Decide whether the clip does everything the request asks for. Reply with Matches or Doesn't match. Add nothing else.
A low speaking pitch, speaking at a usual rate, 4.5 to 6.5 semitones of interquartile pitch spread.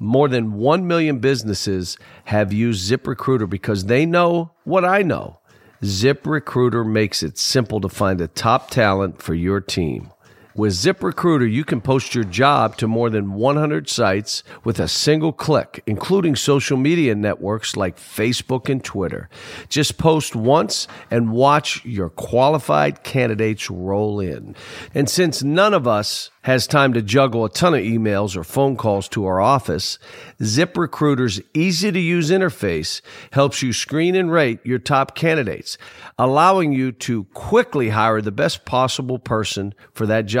Matches